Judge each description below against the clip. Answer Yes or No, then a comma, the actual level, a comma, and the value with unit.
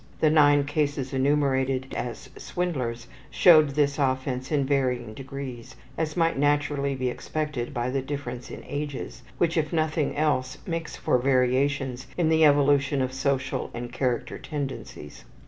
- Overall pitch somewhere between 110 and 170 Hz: Yes, medium, 140 Hz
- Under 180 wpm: Yes, average, 145 wpm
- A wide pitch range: No, narrow, 2.4 semitones